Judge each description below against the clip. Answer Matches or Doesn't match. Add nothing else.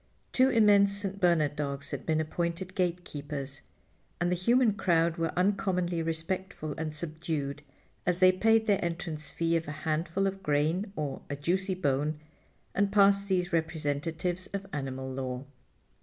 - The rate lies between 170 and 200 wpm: Doesn't match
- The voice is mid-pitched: Matches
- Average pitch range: Matches